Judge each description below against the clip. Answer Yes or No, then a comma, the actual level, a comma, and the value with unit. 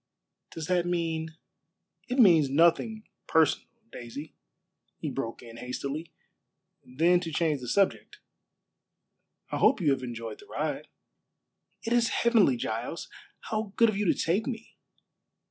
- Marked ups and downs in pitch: Yes, wide, 7.2 semitones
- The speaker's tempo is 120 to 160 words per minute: Yes, average, 140 wpm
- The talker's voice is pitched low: No, medium, 165 Hz